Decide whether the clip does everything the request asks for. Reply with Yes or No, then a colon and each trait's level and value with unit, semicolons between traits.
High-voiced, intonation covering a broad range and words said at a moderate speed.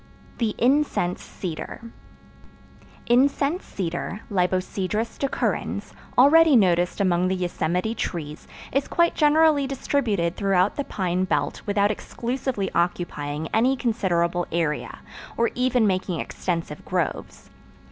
No: high, 200 Hz; wide, 6.3 semitones; slow, 105 wpm